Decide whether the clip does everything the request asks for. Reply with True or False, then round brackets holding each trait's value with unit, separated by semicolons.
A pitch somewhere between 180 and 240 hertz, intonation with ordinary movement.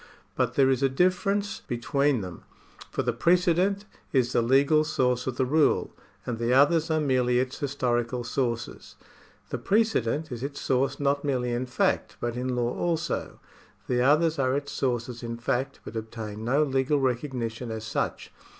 False (130 Hz; 3.3 semitones)